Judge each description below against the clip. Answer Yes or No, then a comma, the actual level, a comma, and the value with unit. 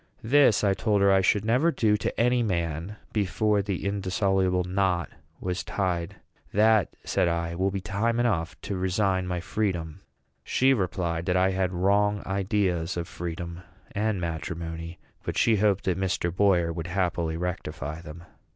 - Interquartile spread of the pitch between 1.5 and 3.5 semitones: Yes, average, 3.1 semitones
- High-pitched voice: No, very low, 95 Hz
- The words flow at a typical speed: Yes, average, 160 wpm